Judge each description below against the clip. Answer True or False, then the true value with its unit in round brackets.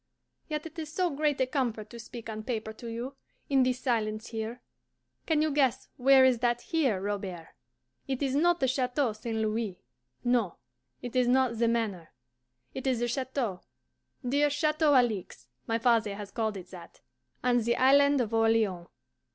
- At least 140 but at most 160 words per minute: False (175 wpm)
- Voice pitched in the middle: False (240 Hz)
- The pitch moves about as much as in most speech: True (3.5 semitones)